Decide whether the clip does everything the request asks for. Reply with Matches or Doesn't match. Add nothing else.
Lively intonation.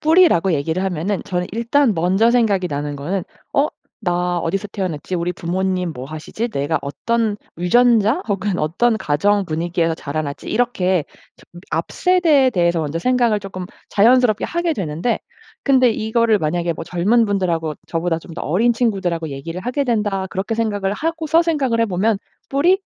Matches